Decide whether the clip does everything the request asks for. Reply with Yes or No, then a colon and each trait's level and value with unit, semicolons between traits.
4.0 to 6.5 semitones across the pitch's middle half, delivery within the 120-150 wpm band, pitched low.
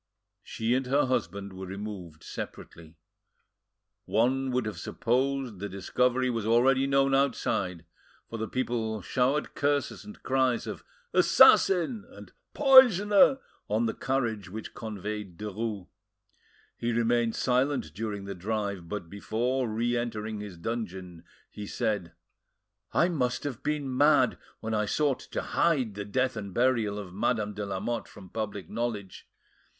Yes: average, 4.3 semitones; average, 140 wpm; low, 115 Hz